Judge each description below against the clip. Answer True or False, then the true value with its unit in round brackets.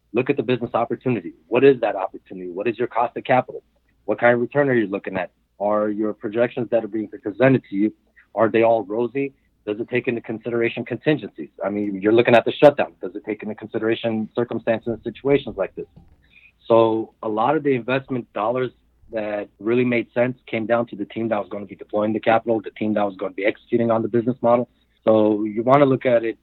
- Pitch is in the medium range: False (115 Hz)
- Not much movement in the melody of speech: True (2.3 semitones)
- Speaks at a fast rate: True (230 wpm)